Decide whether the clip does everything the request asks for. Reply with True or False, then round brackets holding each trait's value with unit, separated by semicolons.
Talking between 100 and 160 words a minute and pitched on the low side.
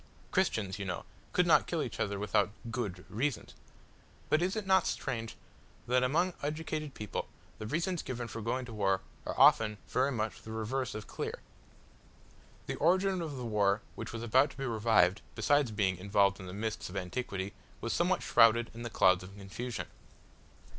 False (180 wpm; 115 Hz)